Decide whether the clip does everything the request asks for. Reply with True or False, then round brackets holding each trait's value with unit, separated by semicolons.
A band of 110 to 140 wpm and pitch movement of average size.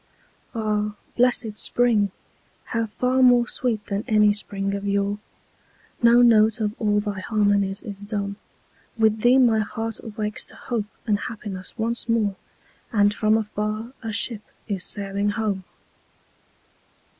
False (135 wpm; 2.0 semitones)